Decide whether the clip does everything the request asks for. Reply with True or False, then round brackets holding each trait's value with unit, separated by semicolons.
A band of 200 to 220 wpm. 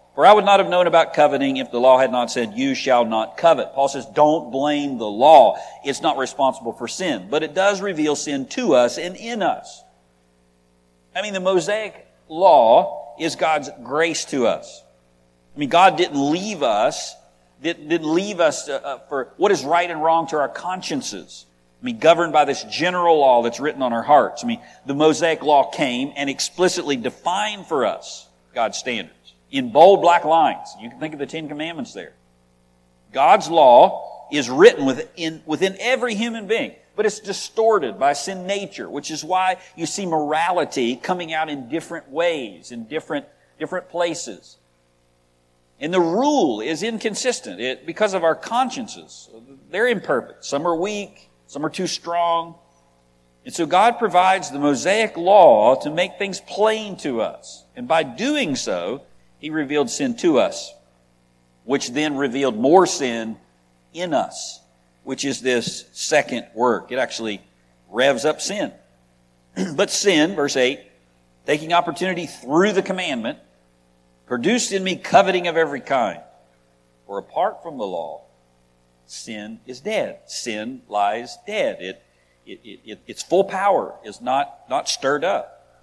False (160 wpm)